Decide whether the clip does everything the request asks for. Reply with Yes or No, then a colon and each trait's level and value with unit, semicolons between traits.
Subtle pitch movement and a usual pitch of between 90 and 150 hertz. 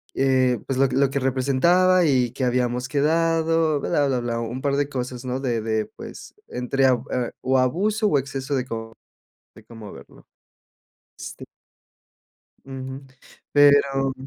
Yes: narrow, 2.3 semitones; low, 135 Hz